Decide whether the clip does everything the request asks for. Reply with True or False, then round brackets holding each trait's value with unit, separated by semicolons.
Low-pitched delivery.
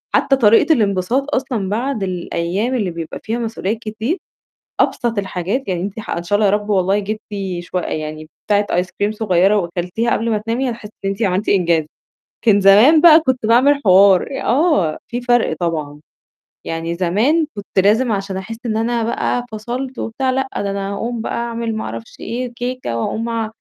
False (215 Hz)